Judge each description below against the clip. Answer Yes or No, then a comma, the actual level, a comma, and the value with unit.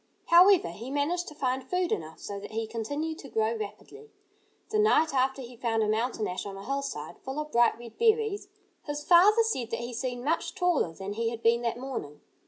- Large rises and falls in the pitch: Yes, wide, 6.2 semitones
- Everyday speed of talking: No, fast, 210 wpm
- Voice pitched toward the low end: No, very high, 255 Hz